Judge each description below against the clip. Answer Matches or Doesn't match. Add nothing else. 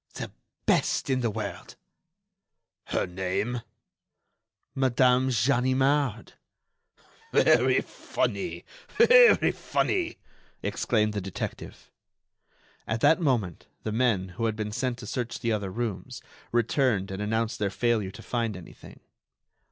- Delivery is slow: Matches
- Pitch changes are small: Doesn't match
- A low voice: Matches